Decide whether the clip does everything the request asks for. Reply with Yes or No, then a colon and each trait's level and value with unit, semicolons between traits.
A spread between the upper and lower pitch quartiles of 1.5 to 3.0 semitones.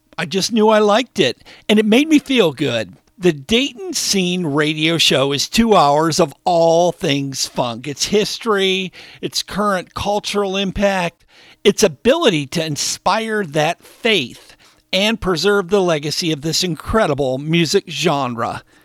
No: average, 4.9 semitones